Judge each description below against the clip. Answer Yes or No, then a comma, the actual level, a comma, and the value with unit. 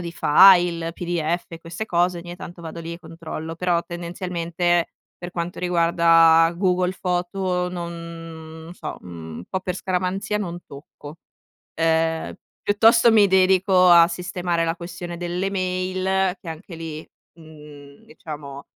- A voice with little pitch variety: Yes, narrow, 1.8 semitones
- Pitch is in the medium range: Yes, medium, 175 Hz